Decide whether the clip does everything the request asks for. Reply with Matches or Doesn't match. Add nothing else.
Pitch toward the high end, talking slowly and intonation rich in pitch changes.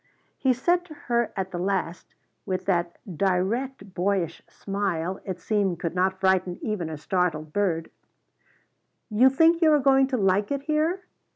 Doesn't match